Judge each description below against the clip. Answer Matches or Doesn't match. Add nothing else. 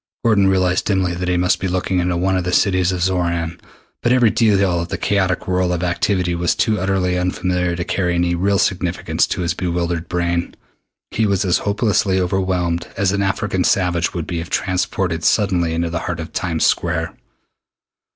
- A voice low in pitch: Matches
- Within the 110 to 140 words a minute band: Doesn't match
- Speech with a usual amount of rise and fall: Doesn't match